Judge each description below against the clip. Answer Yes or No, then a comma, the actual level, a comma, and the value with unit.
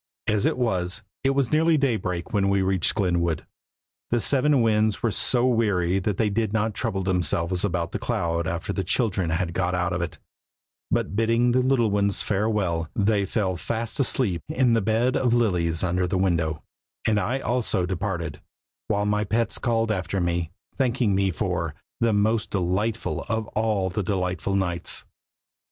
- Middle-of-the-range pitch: No, low, 100 Hz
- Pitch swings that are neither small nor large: Yes, average, 4.0 semitones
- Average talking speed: Yes, average, 170 wpm